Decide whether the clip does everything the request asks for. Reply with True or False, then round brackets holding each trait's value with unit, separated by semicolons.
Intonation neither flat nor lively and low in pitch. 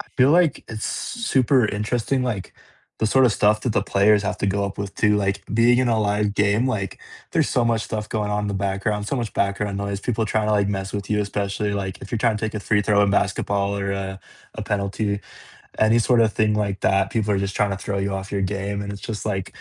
False (1.7 semitones; 105 Hz)